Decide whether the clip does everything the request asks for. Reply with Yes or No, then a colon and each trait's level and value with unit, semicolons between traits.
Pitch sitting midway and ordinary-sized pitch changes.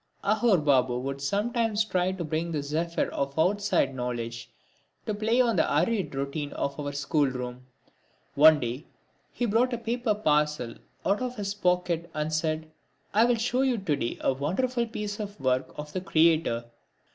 No: medium, 165 Hz; wide, 7.1 semitones